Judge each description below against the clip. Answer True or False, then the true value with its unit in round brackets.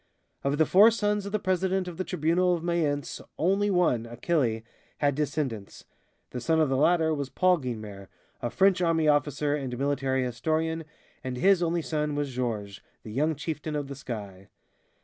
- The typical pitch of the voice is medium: True (150 Hz)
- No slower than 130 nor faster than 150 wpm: False (175 wpm)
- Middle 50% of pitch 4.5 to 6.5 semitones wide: True (5.1 semitones)